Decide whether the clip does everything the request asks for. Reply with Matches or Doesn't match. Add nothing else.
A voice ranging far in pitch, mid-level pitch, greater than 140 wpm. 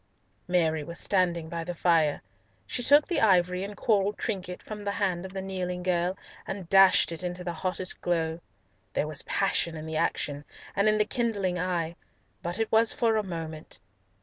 Doesn't match